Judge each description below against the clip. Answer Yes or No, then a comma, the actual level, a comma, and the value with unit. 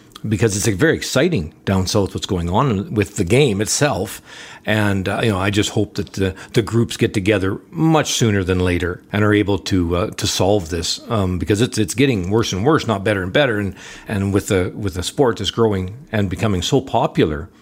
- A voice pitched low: Yes, low, 105 Hz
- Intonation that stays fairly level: No, average, 3.1 semitones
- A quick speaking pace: Yes, fast, 220 wpm